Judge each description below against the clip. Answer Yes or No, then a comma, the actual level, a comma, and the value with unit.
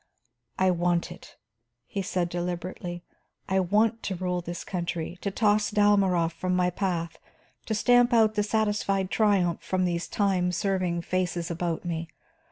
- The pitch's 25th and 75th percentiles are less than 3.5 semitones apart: Yes, average, 2.9 semitones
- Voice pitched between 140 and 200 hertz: Yes, medium, 185 Hz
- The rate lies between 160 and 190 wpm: No, average, 150 wpm